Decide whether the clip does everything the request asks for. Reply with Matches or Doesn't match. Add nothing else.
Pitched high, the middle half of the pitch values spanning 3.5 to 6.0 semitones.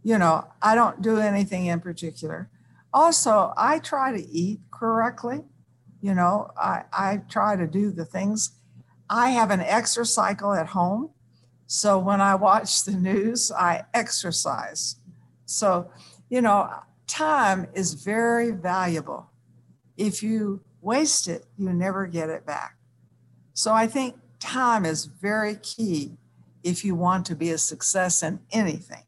Matches